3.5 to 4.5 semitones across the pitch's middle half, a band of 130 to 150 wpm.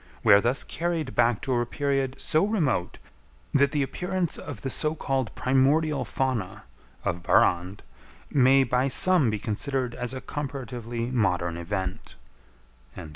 Yes: average, 4.2 semitones; average, 140 wpm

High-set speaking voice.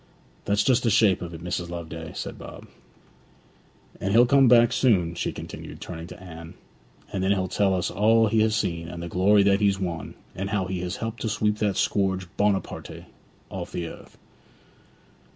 No: very low, 95 Hz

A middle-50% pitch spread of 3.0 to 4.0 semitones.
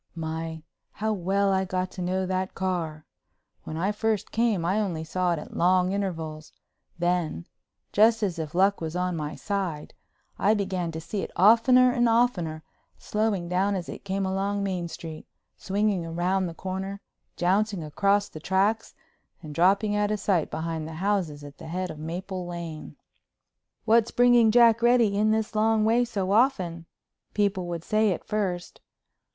Yes: average, 3.7 semitones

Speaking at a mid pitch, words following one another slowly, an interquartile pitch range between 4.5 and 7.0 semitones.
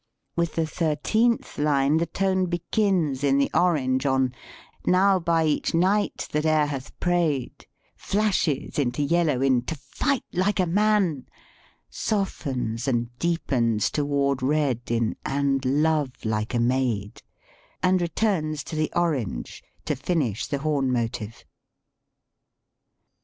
Yes: medium, 150 Hz; slow, 130 wpm; average, 5.0 semitones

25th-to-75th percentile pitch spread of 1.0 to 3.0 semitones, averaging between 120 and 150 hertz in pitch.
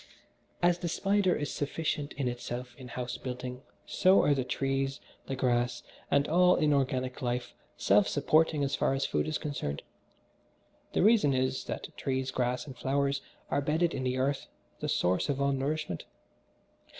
Yes: average, 2.7 semitones; low, 135 Hz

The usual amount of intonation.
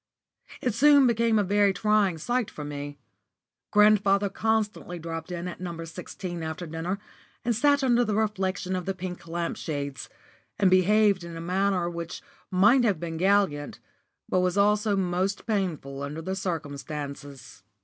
Yes: average, 4.0 semitones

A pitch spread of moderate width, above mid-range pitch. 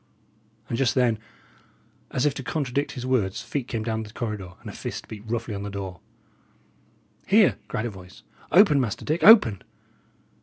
No: average, 4.5 semitones; low, 115 Hz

